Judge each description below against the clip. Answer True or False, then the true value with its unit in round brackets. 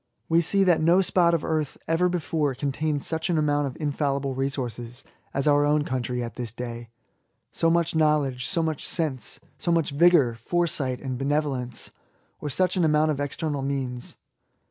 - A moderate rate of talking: True (170 wpm)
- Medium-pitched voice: True (145 Hz)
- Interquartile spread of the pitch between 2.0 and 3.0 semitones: False (3.7 semitones)